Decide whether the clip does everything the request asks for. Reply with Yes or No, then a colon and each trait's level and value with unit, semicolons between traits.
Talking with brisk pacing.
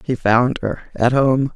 No: average, 195 wpm